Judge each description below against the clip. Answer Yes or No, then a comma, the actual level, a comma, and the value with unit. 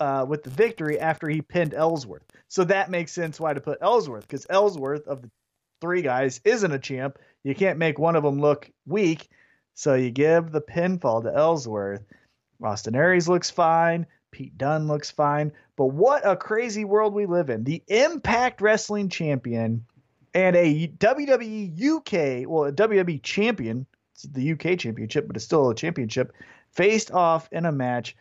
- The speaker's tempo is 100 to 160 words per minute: No, average, 175 wpm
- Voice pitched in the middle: Yes, medium, 160 Hz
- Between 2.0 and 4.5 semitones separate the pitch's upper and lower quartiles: No, wide, 5.5 semitones